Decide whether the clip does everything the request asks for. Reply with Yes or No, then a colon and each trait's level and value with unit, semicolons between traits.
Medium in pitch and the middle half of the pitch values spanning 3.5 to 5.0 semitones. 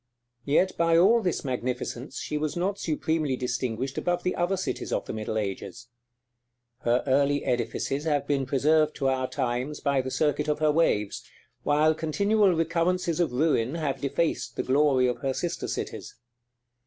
Yes: medium, 145 Hz; average, 4.2 semitones